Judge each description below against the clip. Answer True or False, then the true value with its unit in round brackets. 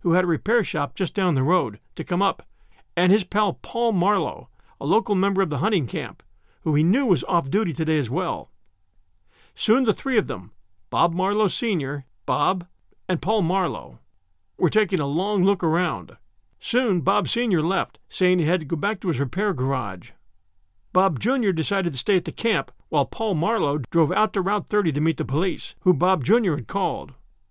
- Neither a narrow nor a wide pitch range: False (5.7 semitones)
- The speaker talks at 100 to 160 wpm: False (195 wpm)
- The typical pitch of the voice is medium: True (180 Hz)